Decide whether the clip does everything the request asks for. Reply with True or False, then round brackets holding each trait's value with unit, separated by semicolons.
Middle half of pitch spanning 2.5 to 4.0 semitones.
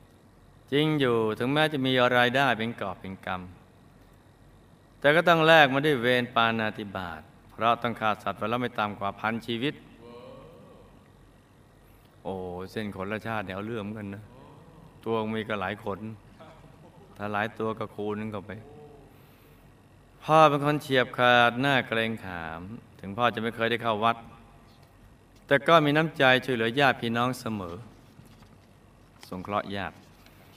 True (3.6 semitones)